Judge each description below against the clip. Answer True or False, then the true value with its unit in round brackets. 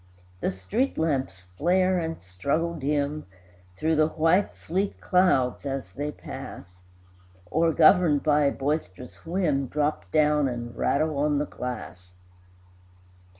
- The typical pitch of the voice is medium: True (150 Hz)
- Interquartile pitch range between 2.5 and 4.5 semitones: True (3.7 semitones)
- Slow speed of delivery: True (125 wpm)